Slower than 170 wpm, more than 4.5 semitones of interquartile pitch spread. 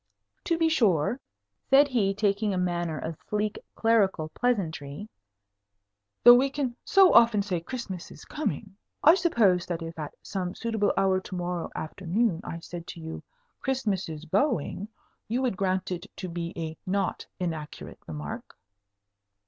Yes: average, 150 wpm; wide, 5.4 semitones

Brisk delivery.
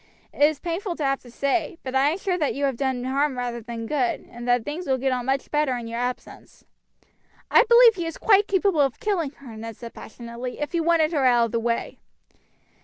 Yes: fast, 235 wpm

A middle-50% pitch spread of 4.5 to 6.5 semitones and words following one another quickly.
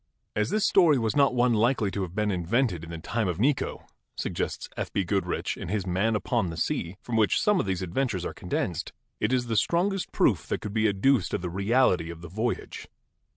Yes: average, 5.3 semitones; fast, 225 wpm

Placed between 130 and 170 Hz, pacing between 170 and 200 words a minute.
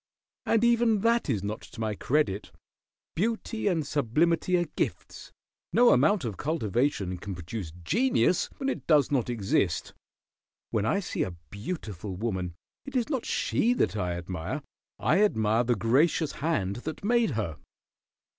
No: low, 135 Hz; average, 150 wpm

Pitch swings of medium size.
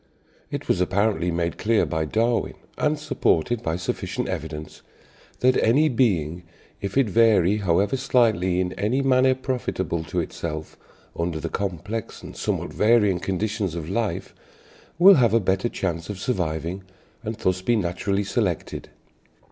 Yes: average, 5.0 semitones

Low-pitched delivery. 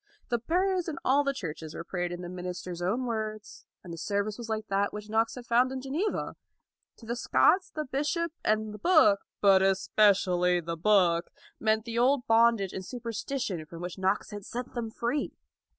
No: high, 215 Hz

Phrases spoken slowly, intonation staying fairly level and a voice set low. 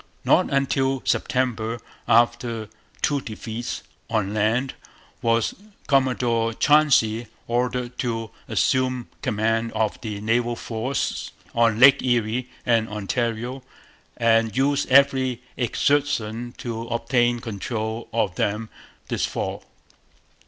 Yes: slow, 105 wpm; narrow, 2.3 semitones; low, 120 Hz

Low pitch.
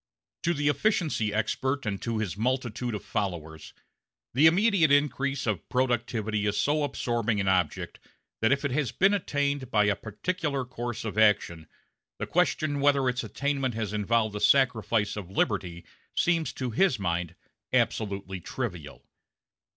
Yes: low, 120 Hz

